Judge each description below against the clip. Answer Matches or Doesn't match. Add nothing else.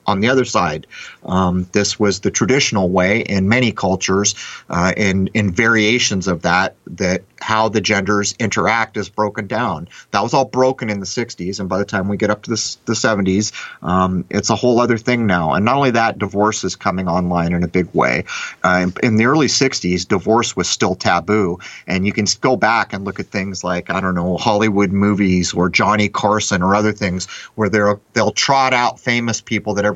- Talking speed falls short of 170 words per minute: Doesn't match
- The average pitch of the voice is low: Matches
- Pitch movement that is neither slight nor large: Matches